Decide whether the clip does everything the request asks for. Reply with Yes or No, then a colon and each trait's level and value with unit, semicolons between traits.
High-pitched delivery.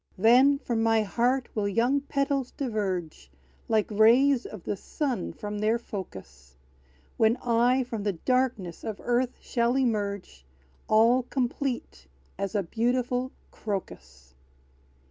Yes: high, 225 Hz